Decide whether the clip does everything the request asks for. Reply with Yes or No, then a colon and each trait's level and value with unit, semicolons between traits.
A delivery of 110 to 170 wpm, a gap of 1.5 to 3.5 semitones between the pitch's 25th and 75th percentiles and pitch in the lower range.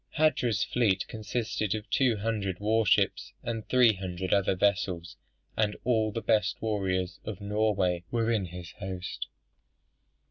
Yes: average, 140 wpm; average, 3.2 semitones; low, 105 Hz